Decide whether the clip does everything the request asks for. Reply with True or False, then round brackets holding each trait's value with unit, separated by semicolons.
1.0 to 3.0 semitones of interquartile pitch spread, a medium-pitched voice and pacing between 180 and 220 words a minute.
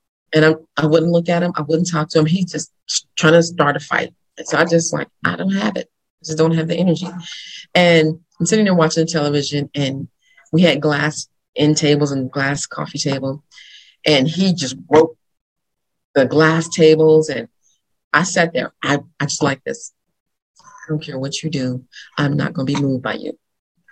True (2.7 semitones; 155 Hz; 205 wpm)